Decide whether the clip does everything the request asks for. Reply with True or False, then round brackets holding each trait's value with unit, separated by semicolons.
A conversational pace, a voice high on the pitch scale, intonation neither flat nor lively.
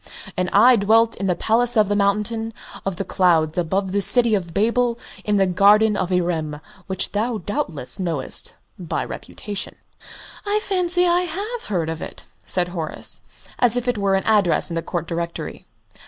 True (175 wpm; 200 Hz; 4.6 semitones)